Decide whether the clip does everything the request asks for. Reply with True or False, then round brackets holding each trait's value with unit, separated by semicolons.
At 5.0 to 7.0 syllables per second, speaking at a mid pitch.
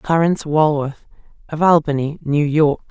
False (4.7 syllables/s; 150 Hz)